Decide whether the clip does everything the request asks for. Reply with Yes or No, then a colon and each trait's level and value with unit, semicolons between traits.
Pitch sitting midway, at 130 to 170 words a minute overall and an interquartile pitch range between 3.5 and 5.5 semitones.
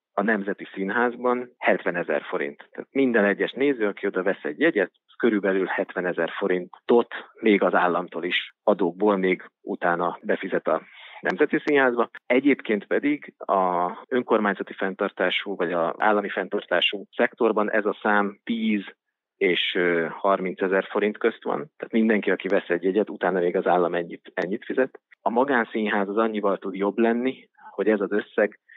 No: low, 105 Hz; fast, 155 wpm; average, 3.9 semitones